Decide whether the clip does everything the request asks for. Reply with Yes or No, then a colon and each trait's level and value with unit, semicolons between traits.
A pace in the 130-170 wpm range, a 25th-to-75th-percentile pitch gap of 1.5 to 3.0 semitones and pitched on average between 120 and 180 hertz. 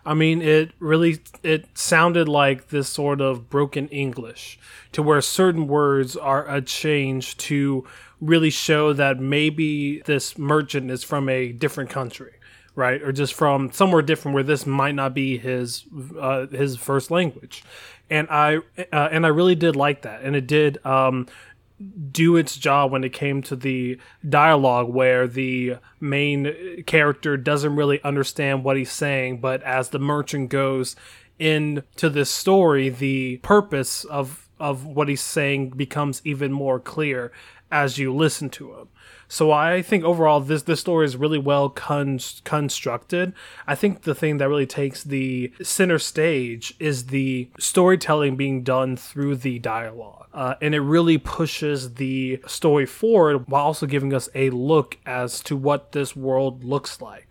Yes: average, 160 wpm; narrow, 2.5 semitones; medium, 140 Hz